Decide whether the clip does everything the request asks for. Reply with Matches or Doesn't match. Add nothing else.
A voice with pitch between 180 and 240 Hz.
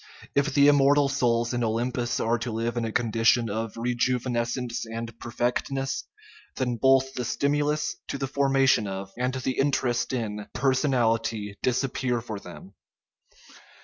Doesn't match